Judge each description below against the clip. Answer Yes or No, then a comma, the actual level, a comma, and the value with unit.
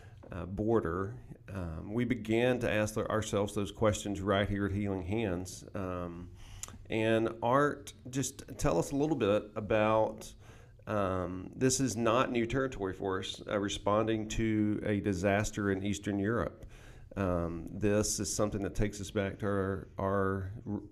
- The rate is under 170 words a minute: Yes, average, 150 wpm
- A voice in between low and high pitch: No, low, 105 Hz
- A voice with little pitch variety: Yes, narrow, 2.2 semitones